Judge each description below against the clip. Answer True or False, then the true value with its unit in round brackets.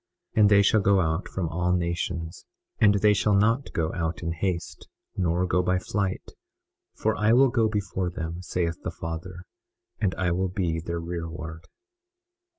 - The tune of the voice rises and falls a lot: False (3.3 semitones)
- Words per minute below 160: False (170 wpm)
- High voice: False (90 Hz)